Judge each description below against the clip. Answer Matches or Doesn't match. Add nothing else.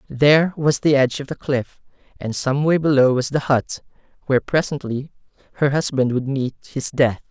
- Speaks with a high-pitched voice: Doesn't match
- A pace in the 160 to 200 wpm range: Matches